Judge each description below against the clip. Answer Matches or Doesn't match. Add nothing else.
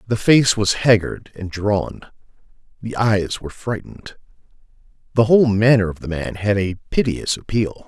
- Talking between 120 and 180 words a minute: Matches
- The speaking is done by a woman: Doesn't match